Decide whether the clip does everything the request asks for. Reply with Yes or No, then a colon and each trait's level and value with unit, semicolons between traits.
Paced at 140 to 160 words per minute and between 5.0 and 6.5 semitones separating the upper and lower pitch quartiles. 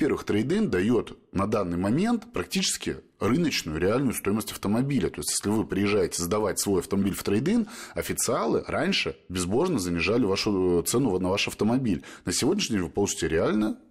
Yes: average, 155 wpm; wide, 5.6 semitones